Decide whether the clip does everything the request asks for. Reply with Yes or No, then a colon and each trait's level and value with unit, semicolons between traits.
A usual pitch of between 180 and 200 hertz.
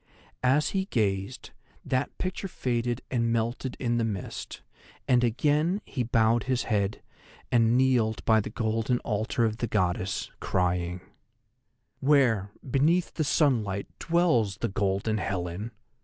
No: low, 115 Hz